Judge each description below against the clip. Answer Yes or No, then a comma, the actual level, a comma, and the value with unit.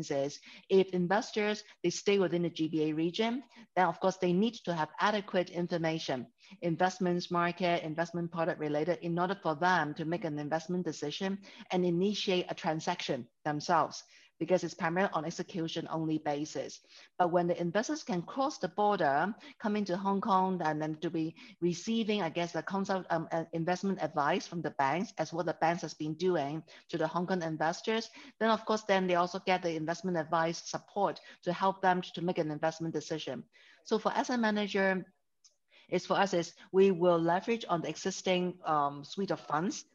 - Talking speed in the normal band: Yes, average, 185 wpm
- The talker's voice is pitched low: No, medium, 175 Hz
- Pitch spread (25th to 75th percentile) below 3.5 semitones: Yes, average, 3.0 semitones